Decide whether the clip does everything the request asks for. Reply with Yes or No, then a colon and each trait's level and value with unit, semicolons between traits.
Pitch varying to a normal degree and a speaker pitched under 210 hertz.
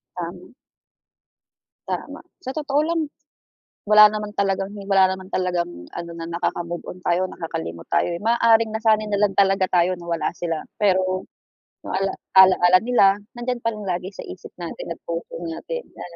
Yes: average, 3.6 semitones; high, 190 Hz